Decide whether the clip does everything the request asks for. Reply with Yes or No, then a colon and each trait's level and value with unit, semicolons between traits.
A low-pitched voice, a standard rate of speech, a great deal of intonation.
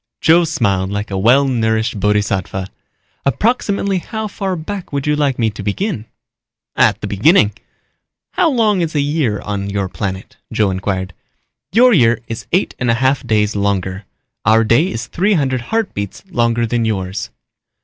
Yes: low, 115 Hz; average, 160 wpm; wide, 8.1 semitones